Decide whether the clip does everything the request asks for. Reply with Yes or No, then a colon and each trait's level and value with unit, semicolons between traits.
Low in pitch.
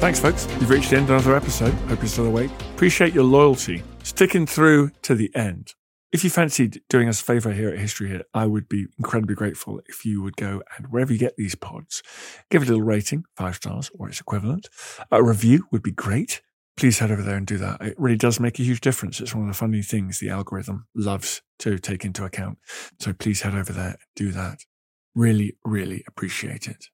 Yes: low, 110 Hz